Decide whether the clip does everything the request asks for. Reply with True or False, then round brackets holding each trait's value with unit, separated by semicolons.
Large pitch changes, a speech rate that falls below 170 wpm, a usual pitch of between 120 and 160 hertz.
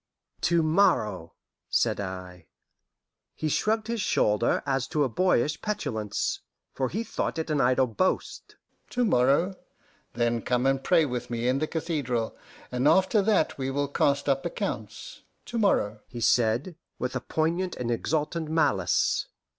True (6.0 semitones; 150 wpm; 140 Hz)